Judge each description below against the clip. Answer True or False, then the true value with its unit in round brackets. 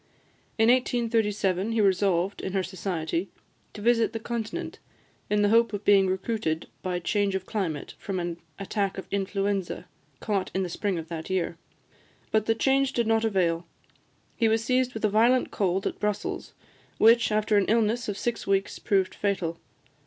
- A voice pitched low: False (205 Hz)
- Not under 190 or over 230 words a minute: False (170 wpm)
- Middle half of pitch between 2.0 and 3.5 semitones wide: True (3.0 semitones)